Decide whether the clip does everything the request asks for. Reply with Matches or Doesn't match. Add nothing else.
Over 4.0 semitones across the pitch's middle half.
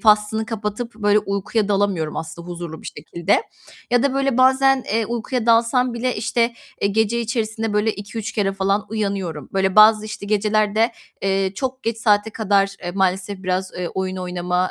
Doesn't match